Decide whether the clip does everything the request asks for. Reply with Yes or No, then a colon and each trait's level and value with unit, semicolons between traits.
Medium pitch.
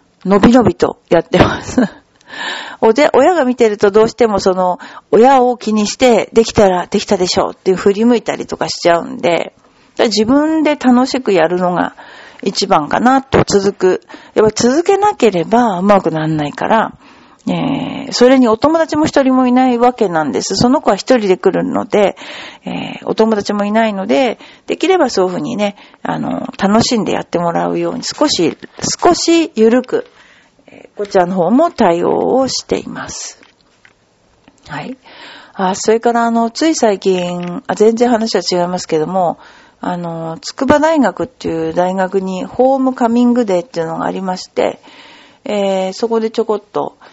No: high, 220 Hz